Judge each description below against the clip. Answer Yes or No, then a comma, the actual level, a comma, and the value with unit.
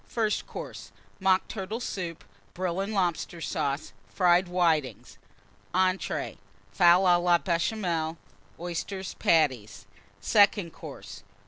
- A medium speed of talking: No, slow, 105 wpm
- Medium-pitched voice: Yes, medium, 175 Hz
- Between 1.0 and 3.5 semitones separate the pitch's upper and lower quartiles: Yes, average, 2.7 semitones